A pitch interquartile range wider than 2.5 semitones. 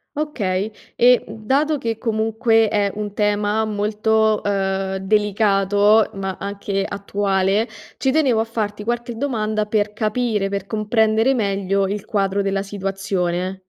No: narrow, 2.0 semitones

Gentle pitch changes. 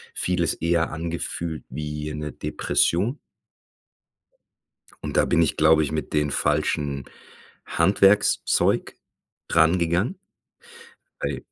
Yes: narrow, 2.3 semitones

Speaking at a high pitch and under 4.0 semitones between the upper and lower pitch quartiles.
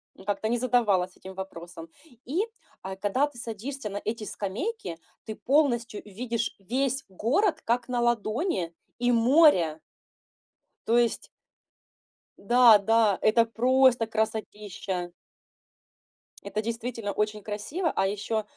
Yes: high, 225 Hz; average, 3.5 semitones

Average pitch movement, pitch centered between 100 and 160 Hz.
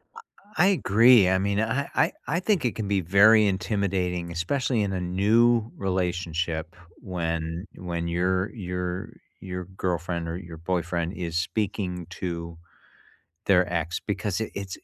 No: average, 3.2 semitones; very low, 90 Hz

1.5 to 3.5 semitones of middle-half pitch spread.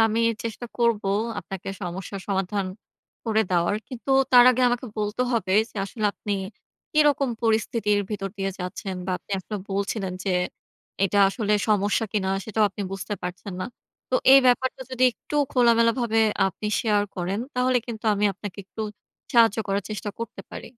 Yes: average, 3.1 semitones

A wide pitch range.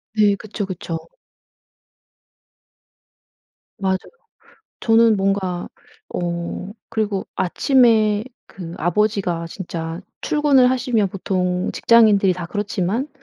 No: average, 3.7 semitones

